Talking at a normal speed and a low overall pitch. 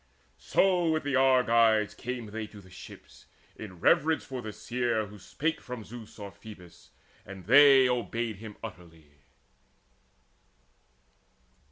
No: slow, 130 wpm; low, 115 Hz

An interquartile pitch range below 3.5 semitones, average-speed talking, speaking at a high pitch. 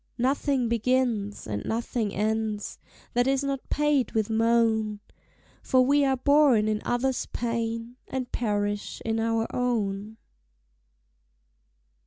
No: average, 2.9 semitones; slow, 115 wpm; high, 230 Hz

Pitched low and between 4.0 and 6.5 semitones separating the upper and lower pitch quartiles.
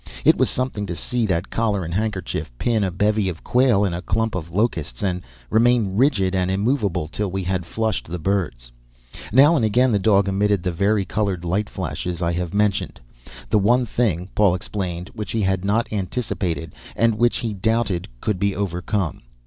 No: low, 100 Hz; average, 3.5 semitones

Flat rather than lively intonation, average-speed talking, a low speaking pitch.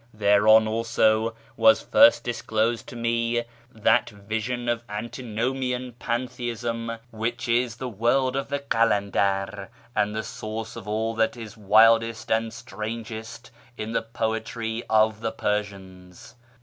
No: narrow, 1.5 semitones; slow, 130 wpm; low, 115 Hz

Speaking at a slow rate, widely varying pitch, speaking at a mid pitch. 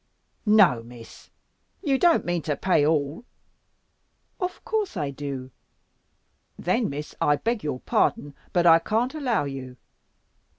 Yes: slow, 130 wpm; wide, 8.4 semitones; medium, 165 Hz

